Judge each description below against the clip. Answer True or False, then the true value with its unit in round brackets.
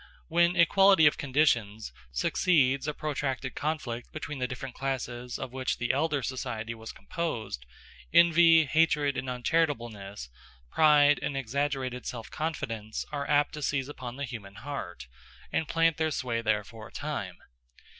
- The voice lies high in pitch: False (135 Hz)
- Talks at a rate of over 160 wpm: False (145 wpm)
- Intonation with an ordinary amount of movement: True (4.4 semitones)